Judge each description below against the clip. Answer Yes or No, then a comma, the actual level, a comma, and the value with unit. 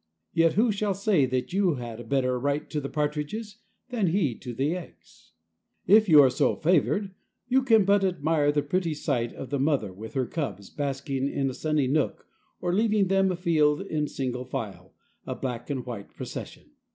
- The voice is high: No, medium, 150 Hz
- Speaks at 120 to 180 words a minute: No, average, 190 wpm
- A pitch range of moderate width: No, wide, 6.3 semitones